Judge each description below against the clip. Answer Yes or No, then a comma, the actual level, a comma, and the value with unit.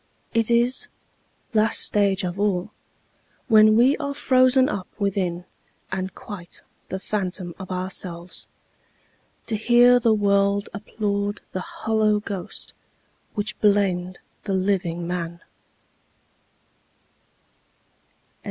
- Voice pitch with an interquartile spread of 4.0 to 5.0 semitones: No, average, 2.9 semitones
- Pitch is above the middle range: Yes, high, 200 Hz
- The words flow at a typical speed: No, slow, 100 wpm